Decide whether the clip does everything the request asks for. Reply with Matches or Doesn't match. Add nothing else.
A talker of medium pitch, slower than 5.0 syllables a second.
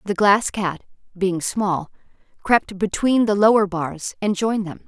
Doesn't match